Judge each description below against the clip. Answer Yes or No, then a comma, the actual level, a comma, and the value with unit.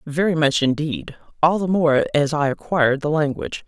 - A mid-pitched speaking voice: Yes, medium, 150 Hz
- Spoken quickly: No, average, 180 wpm